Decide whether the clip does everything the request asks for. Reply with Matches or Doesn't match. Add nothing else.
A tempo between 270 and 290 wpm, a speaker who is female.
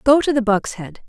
Matches